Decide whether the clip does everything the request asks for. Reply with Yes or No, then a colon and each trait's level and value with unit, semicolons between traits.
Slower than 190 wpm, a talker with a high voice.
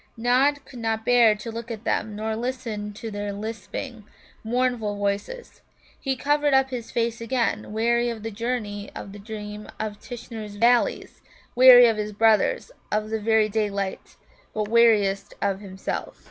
Yes: average, 160 wpm; high, 225 Hz